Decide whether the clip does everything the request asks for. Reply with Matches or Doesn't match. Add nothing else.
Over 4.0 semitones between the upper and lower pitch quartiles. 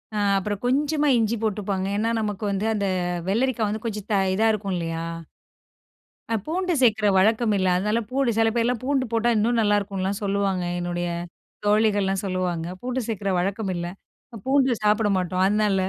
Doesn't match